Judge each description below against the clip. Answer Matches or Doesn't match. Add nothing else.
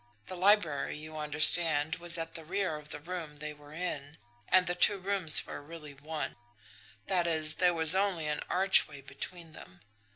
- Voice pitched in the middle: Matches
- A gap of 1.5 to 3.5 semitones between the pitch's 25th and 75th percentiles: Matches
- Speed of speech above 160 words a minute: Matches